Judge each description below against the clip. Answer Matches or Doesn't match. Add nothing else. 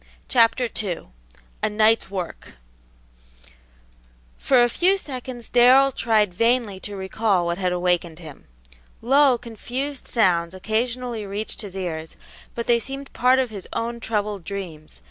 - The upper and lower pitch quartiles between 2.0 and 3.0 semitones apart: Doesn't match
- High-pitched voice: Matches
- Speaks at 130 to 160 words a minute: Matches